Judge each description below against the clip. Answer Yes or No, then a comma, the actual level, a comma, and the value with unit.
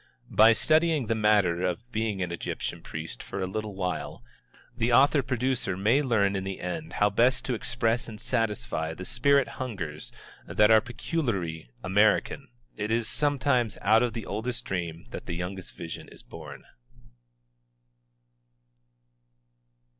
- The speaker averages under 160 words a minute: Yes, average, 145 wpm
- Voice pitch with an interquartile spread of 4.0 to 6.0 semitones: Yes, average, 4.7 semitones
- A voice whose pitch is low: Yes, low, 110 Hz